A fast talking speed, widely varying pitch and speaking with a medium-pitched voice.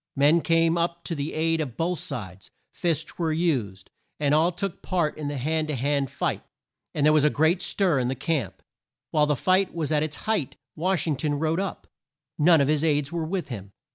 No: fast, 215 wpm; average, 2.8 semitones; medium, 155 Hz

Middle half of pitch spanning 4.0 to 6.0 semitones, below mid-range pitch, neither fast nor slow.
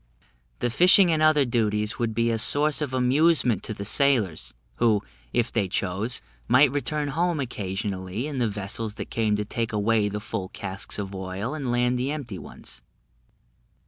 Yes: average, 5.1 semitones; low, 115 Hz; average, 175 wpm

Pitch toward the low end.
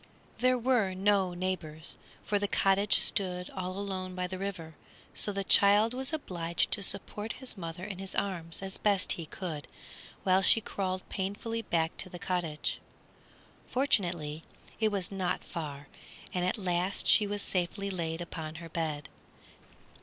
No: medium, 185 Hz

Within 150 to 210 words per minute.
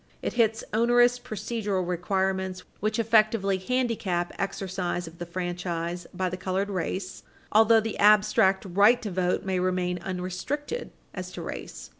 No: average, 140 wpm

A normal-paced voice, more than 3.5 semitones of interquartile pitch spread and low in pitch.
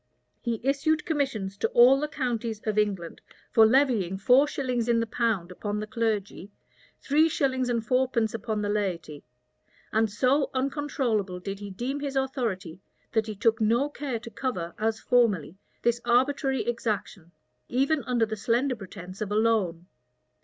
No: average, 160 wpm; average, 4.1 semitones; high, 230 Hz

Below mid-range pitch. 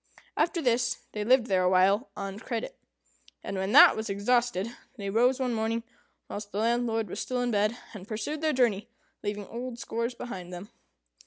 No: high, 225 Hz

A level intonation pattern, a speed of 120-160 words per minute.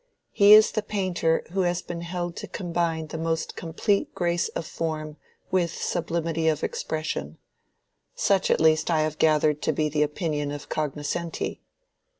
Yes: narrow, 2.0 semitones; average, 155 wpm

